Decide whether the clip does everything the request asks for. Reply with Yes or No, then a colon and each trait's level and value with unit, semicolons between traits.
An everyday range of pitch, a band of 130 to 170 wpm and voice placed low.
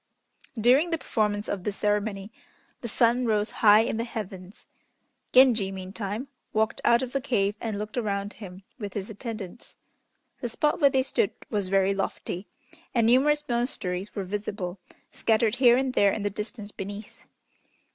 No: average, 3.2 semitones; average, 160 wpm; high, 215 Hz